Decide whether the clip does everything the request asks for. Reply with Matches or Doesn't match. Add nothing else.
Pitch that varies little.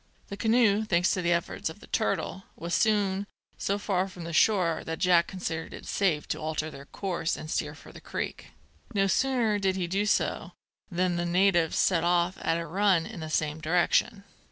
Doesn't match